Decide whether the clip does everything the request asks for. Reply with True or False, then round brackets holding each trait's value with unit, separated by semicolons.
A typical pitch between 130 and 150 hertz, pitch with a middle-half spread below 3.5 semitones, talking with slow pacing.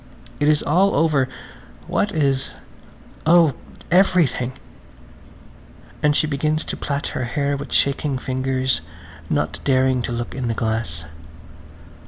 True (140 Hz; 2.9 semitones; 125 wpm)